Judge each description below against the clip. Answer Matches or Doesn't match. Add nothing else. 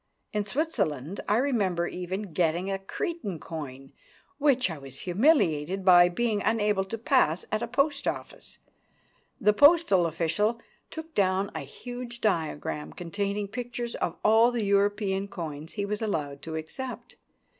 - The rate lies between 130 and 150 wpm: Matches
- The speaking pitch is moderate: Doesn't match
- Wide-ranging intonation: Matches